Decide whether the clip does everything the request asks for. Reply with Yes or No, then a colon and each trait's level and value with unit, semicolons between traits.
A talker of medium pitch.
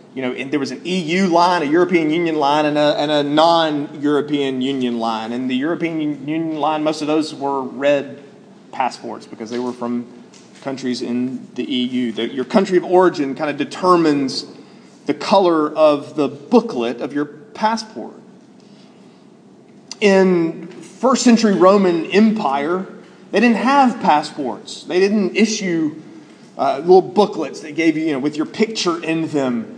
Yes: medium, 165 Hz